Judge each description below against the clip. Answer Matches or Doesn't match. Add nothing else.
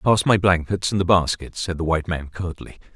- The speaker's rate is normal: Doesn't match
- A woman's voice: Doesn't match